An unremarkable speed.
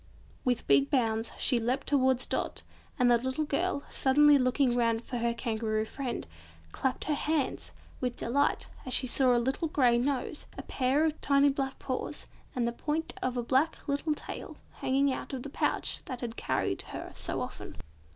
Yes: average, 180 wpm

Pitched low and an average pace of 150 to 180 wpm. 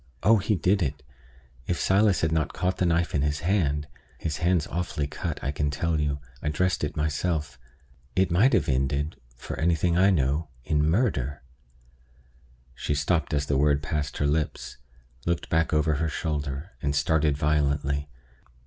Yes: very low, 75 Hz; average, 170 wpm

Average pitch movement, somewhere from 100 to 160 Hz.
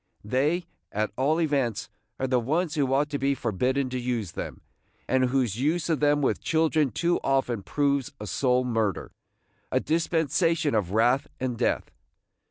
Yes: average, 3.7 semitones; low, 135 Hz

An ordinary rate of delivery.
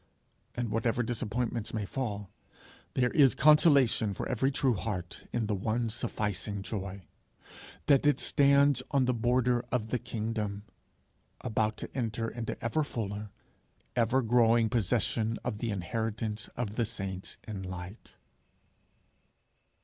No: slow, 130 wpm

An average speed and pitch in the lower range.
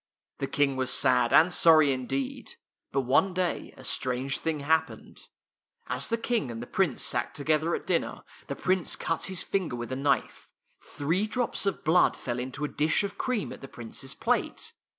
No: average, 185 wpm; medium, 145 Hz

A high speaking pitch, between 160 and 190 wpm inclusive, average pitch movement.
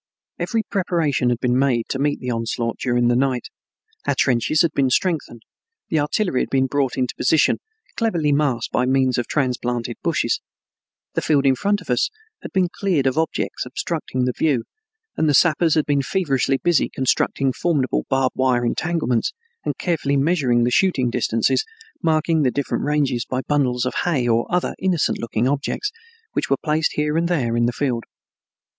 No: low, 135 Hz; average, 175 wpm; average, 4.2 semitones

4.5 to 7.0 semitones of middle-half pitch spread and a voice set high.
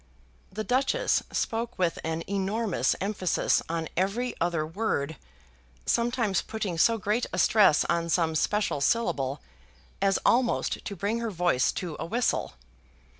Yes: average, 5.2 semitones; high, 195 Hz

